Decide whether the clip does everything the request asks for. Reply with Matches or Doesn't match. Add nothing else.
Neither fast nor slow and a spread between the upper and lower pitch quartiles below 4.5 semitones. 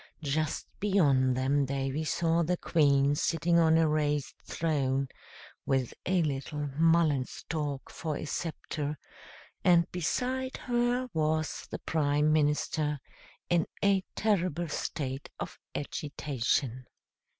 Doesn't match